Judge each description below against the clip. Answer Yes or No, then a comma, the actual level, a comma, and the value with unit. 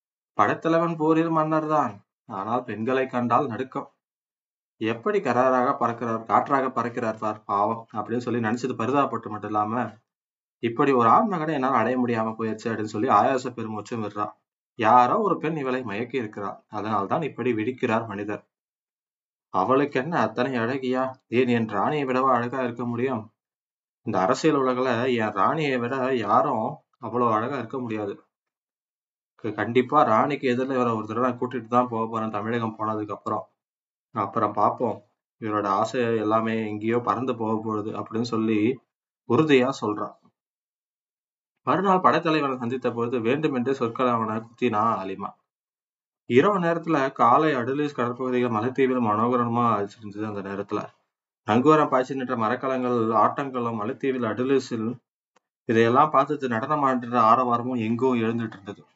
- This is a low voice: Yes, low, 120 Hz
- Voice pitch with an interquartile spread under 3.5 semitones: Yes, average, 2.9 semitones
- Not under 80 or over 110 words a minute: No, average, 125 wpm